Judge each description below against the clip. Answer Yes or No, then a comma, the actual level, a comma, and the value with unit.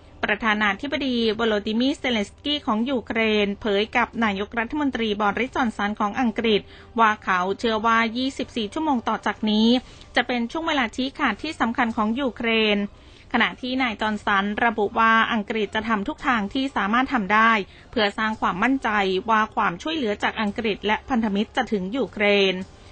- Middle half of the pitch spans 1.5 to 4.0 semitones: Yes, average, 3.0 semitones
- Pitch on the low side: No, high, 225 Hz